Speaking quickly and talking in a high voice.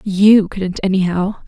No: slow, 120 wpm; high, 195 Hz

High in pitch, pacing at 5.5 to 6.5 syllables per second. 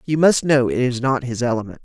No: low, 135 Hz; 5.8 syllables/s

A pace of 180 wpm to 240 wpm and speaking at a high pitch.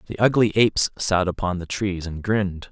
No: average, 200 wpm; very low, 95 Hz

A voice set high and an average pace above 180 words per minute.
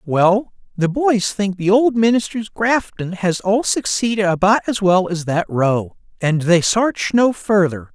No: high, 200 Hz; average, 165 wpm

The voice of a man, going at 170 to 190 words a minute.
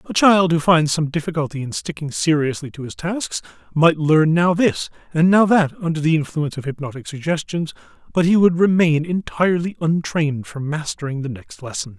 Yes: male; average, 180 wpm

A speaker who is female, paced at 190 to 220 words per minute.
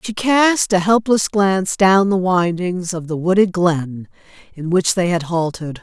No: female; average, 175 wpm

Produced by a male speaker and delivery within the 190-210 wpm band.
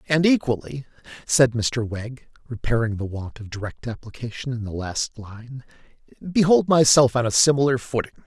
No: male; average, 150 wpm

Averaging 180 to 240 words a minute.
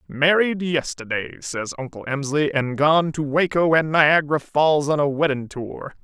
No: average, 160 wpm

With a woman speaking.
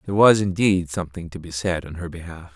No: male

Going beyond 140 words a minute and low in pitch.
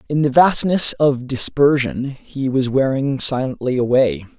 No: slow, 135 wpm; low, 130 Hz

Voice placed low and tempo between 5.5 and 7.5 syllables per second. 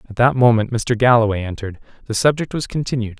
Yes: low, 120 Hz; 6.5 syllables/s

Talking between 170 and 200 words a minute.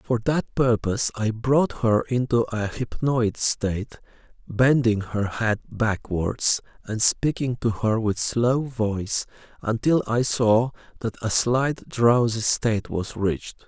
No: slow, 135 wpm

